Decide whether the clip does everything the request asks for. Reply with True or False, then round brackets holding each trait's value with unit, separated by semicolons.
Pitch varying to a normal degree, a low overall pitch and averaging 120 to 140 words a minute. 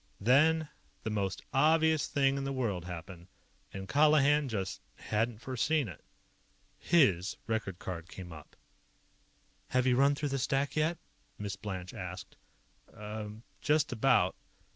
False (6.7 semitones; 115 Hz; 135 wpm)